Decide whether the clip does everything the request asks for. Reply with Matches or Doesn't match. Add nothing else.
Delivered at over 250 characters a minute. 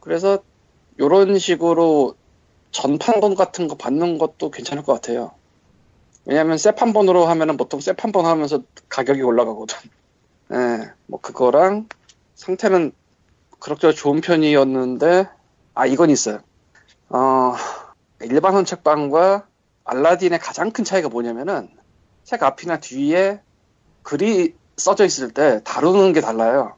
Matches